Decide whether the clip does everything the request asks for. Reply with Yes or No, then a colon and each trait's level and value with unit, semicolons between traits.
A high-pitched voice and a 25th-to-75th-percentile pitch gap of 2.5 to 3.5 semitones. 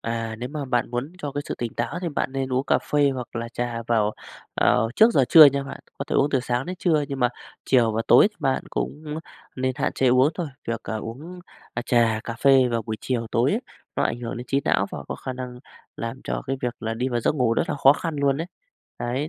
No: low, 130 Hz; average, 3.2 semitones